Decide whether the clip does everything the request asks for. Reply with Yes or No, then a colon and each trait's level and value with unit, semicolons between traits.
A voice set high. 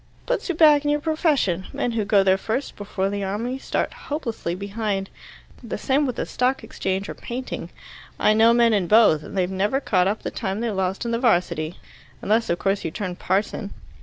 Yes: high, 210 Hz